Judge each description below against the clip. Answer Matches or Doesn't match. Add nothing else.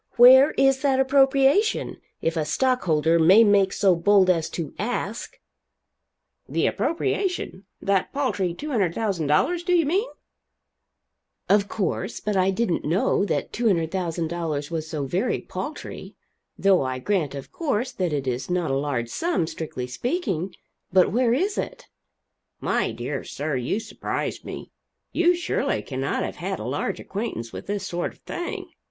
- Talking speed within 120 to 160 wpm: Matches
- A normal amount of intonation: Doesn't match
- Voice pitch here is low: Doesn't match